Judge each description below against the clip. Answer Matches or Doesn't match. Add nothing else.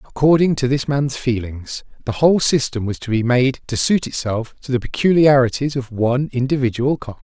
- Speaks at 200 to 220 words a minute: Doesn't match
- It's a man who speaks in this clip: Matches